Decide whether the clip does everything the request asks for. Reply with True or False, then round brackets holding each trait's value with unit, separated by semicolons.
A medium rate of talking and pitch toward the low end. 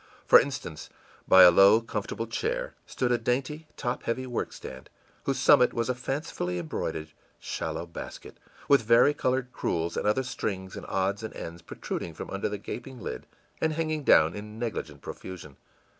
True (160 wpm; 115 Hz)